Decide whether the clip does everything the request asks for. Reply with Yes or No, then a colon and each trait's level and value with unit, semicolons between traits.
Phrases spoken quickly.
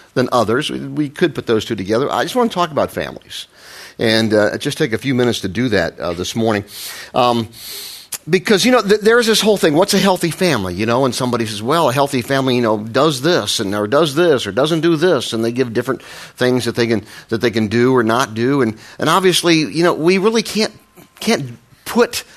Yes: fast, 235 wpm